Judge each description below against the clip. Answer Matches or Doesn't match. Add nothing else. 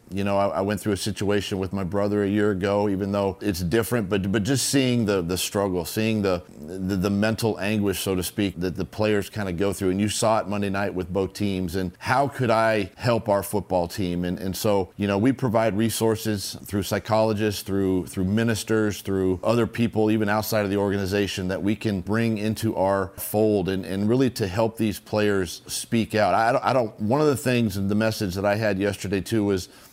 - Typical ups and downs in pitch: Doesn't match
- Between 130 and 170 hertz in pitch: Doesn't match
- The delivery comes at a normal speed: Doesn't match